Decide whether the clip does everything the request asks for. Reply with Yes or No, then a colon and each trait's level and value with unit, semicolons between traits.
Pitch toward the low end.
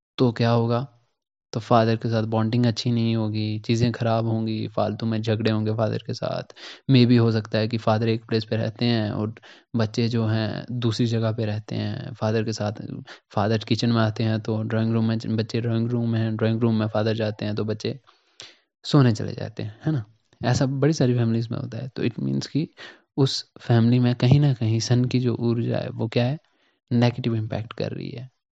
Yes: low, 115 Hz